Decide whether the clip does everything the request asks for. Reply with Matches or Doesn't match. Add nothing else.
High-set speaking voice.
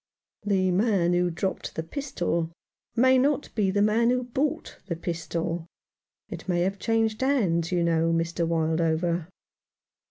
Doesn't match